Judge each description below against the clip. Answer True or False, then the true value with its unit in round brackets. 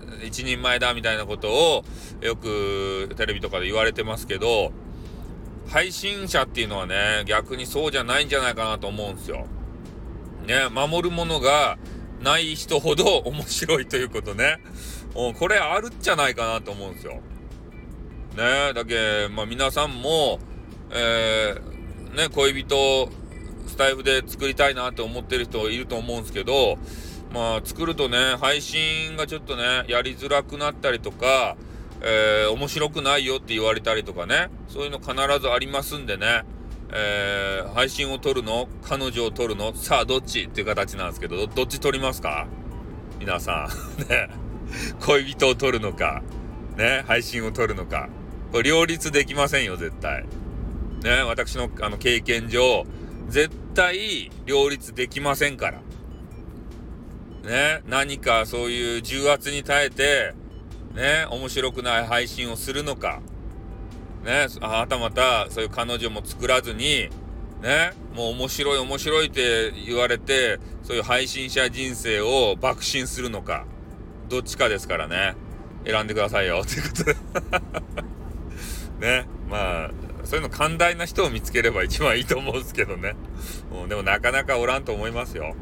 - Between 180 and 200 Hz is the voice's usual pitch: False (120 Hz)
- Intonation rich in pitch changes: False (4.5 semitones)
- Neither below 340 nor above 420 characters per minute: False (300 characters per minute)